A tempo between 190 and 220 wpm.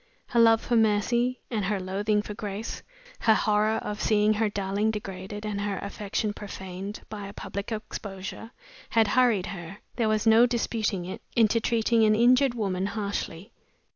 No: average, 165 wpm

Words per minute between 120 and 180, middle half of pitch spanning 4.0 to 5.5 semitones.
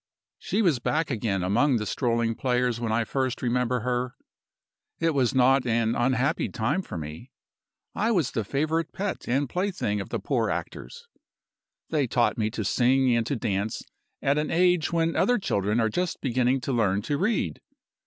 Yes: average, 175 wpm; average, 4.9 semitones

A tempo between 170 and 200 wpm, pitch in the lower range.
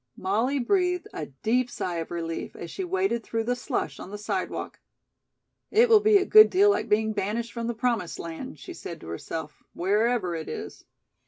No: average, 190 wpm; high, 230 Hz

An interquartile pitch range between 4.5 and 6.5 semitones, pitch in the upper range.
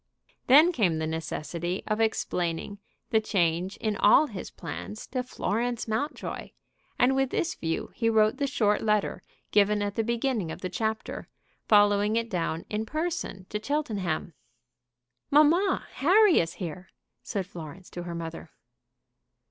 Yes: wide, 5.6 semitones; high, 210 Hz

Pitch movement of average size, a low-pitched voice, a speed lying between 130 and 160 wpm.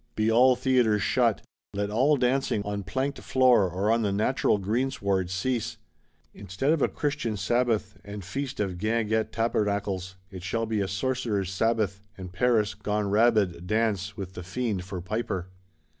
Yes: average, 3.6 semitones; low, 105 Hz; average, 155 wpm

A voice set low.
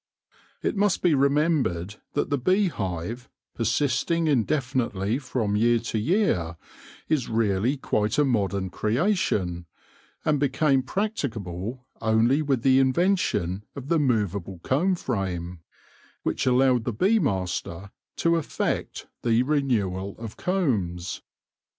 Yes: low, 120 Hz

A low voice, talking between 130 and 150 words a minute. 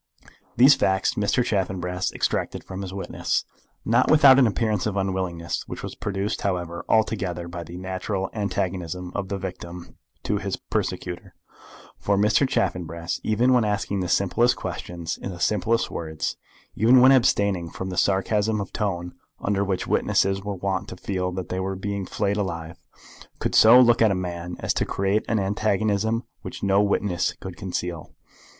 No: very low, 95 Hz; average, 165 wpm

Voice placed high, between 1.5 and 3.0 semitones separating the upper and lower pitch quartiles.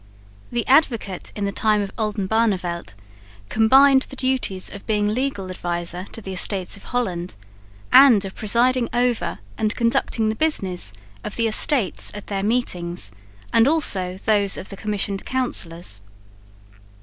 No: high, 210 Hz; average, 4.3 semitones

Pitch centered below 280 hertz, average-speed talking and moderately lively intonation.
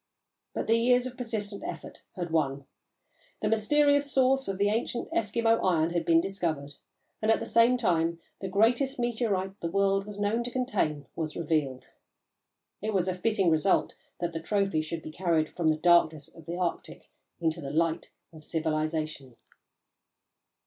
No: medium, 185 Hz; average, 165 wpm; wide, 5.7 semitones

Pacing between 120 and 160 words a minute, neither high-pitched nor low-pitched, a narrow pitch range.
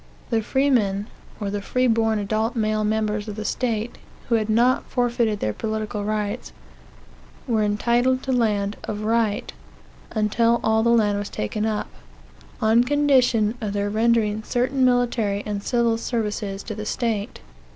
No: average, 150 wpm; high, 220 Hz; narrow, 2.2 semitones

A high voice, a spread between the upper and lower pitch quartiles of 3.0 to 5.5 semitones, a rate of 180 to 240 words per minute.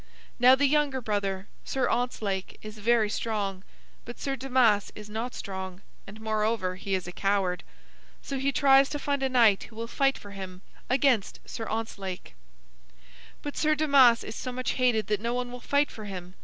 Yes: high, 225 Hz; average, 4.6 semitones; average, 185 wpm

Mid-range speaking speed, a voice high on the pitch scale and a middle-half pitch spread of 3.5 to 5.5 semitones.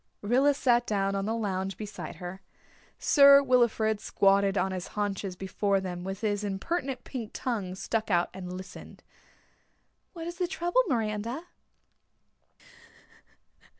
No: slow, 130 wpm; high, 210 Hz; average, 4.5 semitones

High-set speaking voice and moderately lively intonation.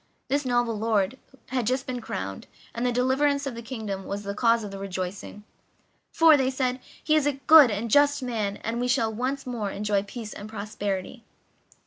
Yes: high, 235 Hz; average, 4.1 semitones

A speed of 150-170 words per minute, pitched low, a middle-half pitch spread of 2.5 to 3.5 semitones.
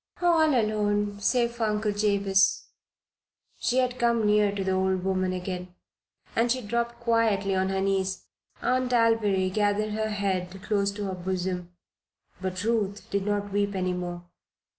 No: average, 155 wpm; high, 205 Hz; average, 2.8 semitones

